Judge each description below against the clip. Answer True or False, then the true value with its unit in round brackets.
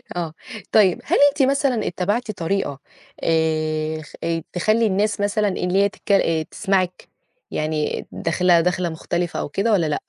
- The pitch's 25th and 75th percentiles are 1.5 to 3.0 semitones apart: False (4.1 semitones)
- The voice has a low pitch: False (180 Hz)